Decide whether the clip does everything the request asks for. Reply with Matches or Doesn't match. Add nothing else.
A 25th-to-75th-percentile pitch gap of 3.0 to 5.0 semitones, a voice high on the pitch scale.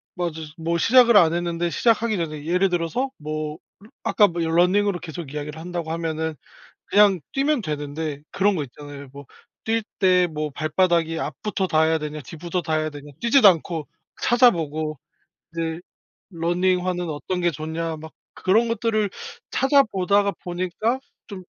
Doesn't match